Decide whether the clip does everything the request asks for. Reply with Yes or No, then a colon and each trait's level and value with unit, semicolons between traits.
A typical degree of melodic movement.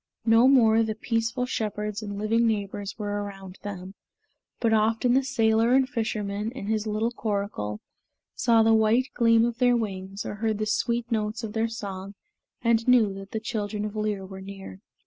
No: narrow, 2.1 semitones